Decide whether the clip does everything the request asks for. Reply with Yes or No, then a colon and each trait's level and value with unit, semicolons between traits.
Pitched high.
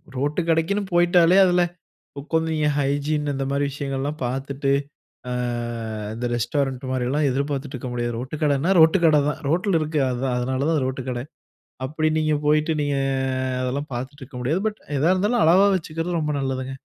No: medium, 145 Hz